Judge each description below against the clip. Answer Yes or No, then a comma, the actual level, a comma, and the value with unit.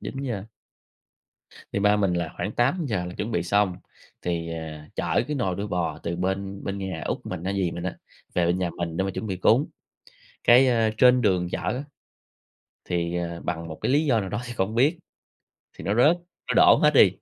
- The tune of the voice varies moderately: Yes, average, 4.9 semitones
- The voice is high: No, very low, 95 Hz